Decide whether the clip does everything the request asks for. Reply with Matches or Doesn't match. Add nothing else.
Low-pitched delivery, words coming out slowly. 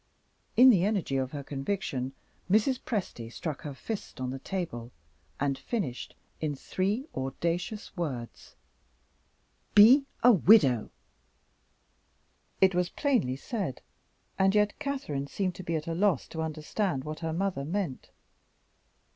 Doesn't match